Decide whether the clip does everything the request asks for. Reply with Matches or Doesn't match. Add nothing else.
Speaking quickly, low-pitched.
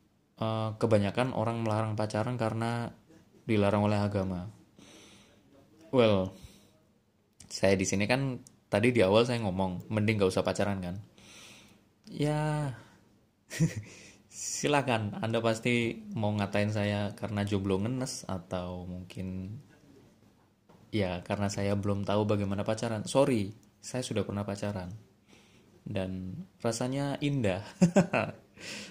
Doesn't match